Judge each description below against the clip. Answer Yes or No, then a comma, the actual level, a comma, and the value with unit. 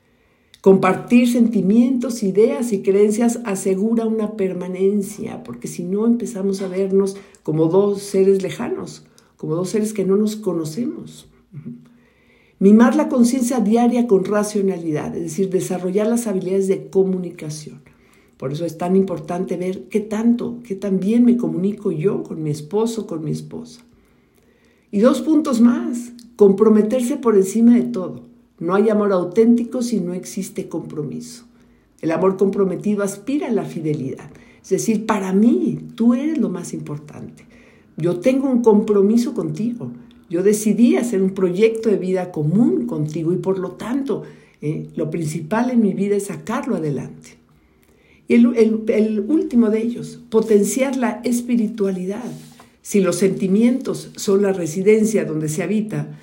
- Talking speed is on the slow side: No, average, 145 wpm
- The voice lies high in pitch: Yes, high, 200 Hz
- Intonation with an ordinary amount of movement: Yes, average, 3.7 semitones